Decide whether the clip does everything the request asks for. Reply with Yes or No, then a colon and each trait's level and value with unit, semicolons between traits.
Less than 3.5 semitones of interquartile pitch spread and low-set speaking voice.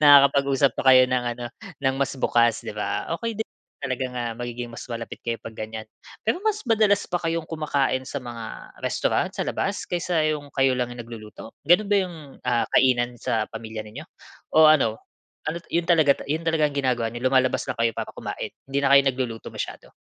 No: average, 4.9 semitones; low, 130 Hz